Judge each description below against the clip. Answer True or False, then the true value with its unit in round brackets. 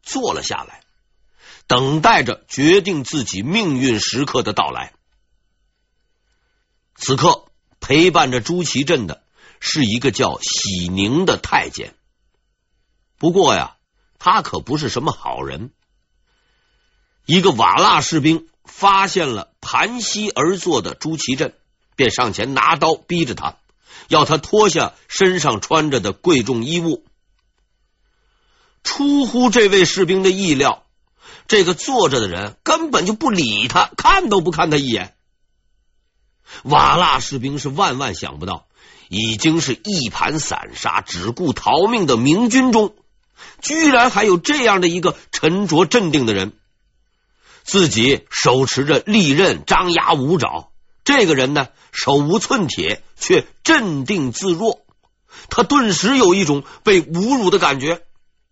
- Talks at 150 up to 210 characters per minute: True (195 characters per minute)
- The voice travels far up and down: True (7.6 semitones)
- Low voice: False (165 Hz)